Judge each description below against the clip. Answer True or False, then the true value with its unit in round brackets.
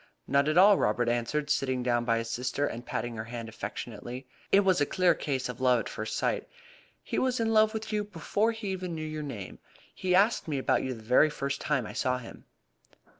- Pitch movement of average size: False (7.3 semitones)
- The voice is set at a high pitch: False (140 Hz)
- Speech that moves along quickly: True (225 wpm)